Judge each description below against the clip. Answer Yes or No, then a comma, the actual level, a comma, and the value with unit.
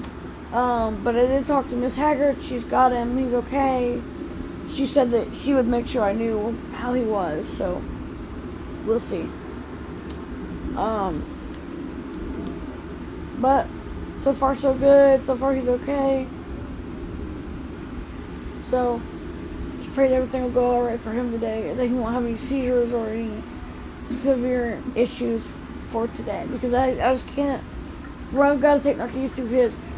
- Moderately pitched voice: No, high, 245 Hz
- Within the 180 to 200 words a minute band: No, average, 150 wpm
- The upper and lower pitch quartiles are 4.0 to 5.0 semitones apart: No, average, 2.7 semitones